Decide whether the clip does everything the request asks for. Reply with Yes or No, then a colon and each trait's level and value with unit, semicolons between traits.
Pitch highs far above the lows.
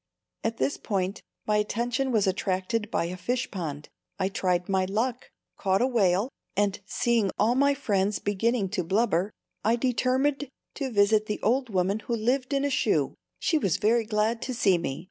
No: average, 4.1 semitones